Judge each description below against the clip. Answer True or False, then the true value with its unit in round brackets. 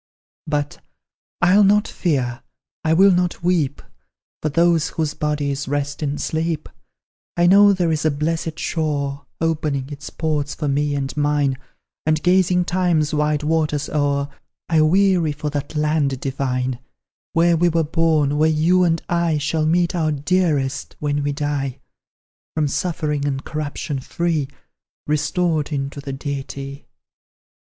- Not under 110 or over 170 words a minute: True (140 wpm)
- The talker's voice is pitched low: False (150 Hz)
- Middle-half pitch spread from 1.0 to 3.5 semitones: True (2.6 semitones)